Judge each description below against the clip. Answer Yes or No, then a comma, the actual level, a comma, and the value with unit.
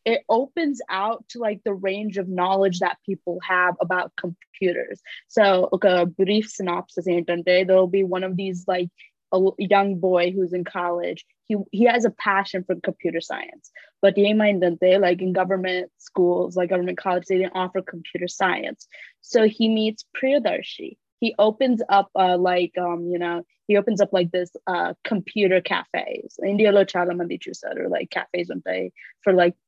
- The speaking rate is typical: Yes, average, 170 wpm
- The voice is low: No, high, 190 Hz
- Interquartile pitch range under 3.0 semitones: Yes, narrow, 2.4 semitones